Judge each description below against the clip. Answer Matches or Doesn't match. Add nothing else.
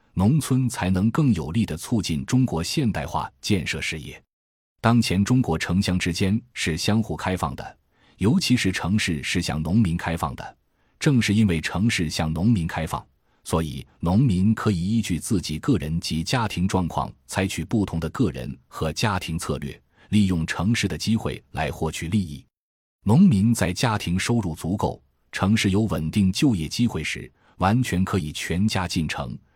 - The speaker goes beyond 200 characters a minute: Matches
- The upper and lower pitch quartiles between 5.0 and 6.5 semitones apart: Matches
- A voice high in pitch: Doesn't match